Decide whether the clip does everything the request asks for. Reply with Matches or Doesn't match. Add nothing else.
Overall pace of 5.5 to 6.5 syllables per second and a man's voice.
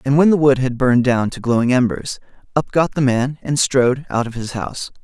Matches